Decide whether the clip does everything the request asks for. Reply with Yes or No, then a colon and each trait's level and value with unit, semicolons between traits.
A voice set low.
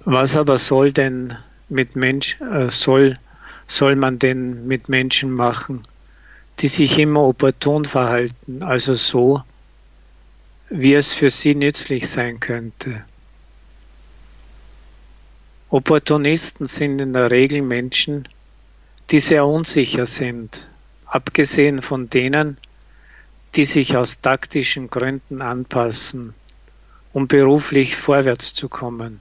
Yes: low, 130 Hz